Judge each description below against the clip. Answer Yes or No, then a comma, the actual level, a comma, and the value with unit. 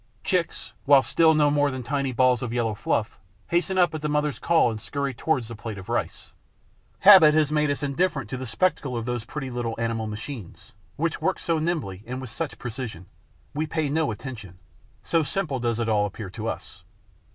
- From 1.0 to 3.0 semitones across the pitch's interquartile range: No, average, 5.0 semitones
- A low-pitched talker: Yes, low, 130 Hz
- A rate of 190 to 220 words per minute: Yes, average, 200 wpm